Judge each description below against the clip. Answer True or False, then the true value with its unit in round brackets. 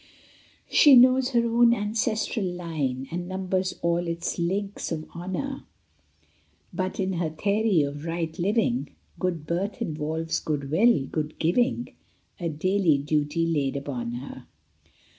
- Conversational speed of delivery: False (130 wpm)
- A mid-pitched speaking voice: True (175 Hz)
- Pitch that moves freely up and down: False (4.9 semitones)